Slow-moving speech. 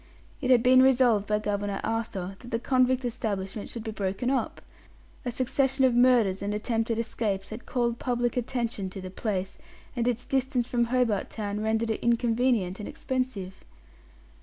No: average, 165 wpm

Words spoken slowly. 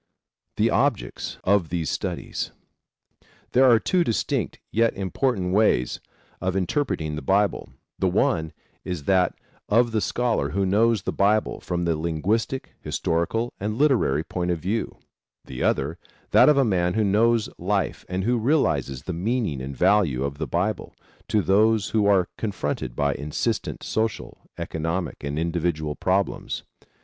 No: average, 150 wpm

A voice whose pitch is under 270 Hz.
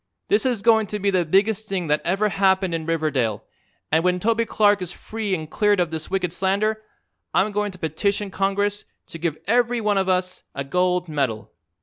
Yes: high, 190 Hz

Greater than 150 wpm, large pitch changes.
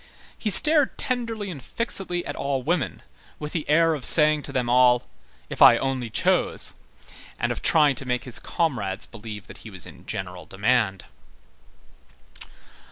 Yes: average, 160 wpm; wide, 6.4 semitones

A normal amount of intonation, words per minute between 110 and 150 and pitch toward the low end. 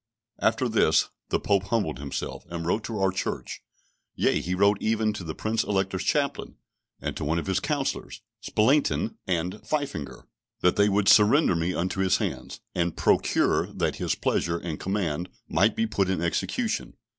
No: average, 3.8 semitones; average, 170 wpm; very low, 95 Hz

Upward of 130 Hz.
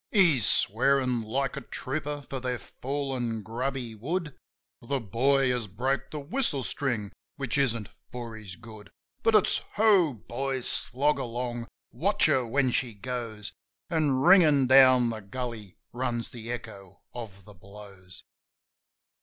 No: low, 125 Hz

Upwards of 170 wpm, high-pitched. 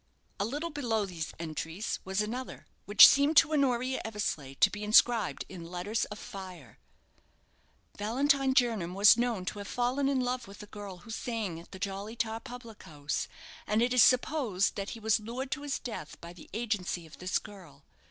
Yes: average, 190 wpm; high, 215 Hz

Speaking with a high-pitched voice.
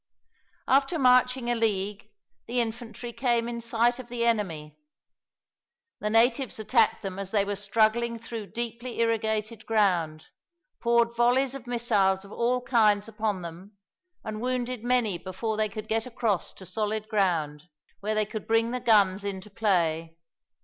Yes: high, 220 Hz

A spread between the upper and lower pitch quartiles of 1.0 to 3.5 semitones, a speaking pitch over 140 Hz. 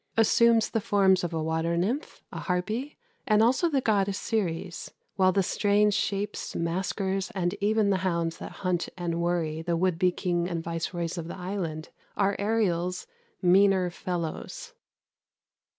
Yes: average, 3.2 semitones; medium, 185 Hz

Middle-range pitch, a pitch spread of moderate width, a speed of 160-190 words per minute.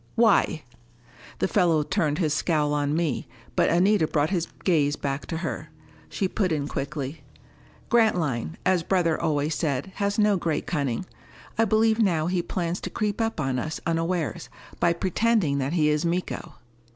Yes: medium, 165 Hz; average, 4.2 semitones; average, 165 wpm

